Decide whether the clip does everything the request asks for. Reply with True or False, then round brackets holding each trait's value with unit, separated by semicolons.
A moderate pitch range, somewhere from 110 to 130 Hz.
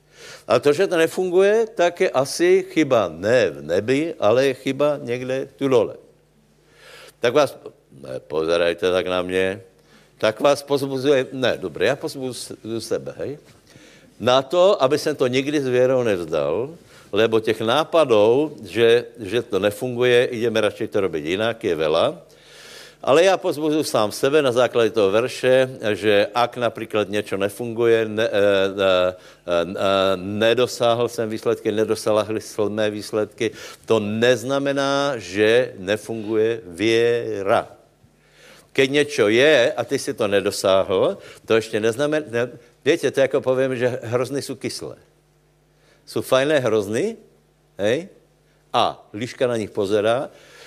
True (4.8 semitones; 120 Hz)